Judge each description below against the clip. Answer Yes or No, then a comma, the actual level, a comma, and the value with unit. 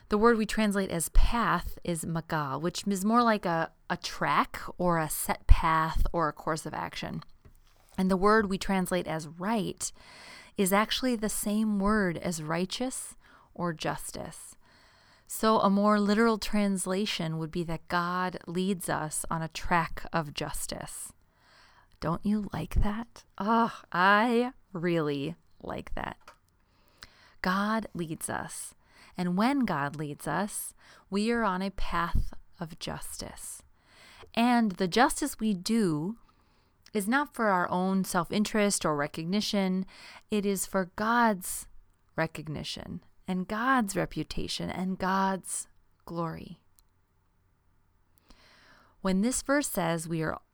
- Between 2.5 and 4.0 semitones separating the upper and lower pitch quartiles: No, average, 4.6 semitones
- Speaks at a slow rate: Yes, slow, 130 wpm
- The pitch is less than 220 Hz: Yes, medium, 185 Hz